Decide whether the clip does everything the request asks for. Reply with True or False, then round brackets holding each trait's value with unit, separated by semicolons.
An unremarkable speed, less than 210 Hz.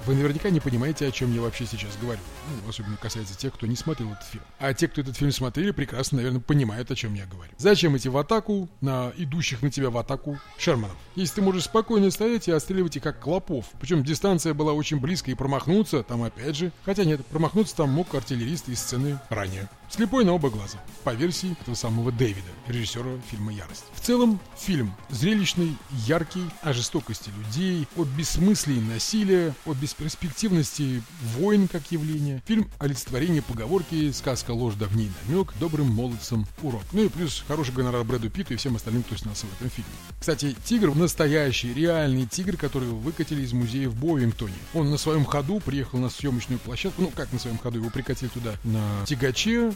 False (190 wpm; 140 Hz)